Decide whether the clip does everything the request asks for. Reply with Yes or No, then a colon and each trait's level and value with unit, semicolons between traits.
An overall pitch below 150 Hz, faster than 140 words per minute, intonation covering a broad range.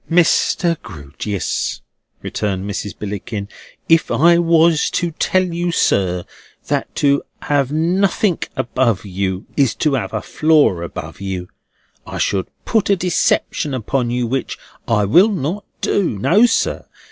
No: low, 135 Hz; slow, 135 wpm; wide, 9.0 semitones